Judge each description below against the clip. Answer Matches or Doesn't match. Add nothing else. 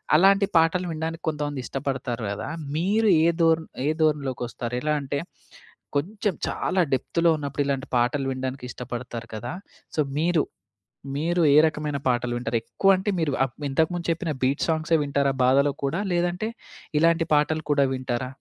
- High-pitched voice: Doesn't match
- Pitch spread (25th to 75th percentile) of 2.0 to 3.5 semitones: Doesn't match